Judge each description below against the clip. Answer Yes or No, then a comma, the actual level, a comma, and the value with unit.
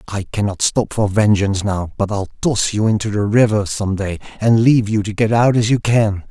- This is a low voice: Yes, low, 105 Hz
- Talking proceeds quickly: Yes, fast, 230 wpm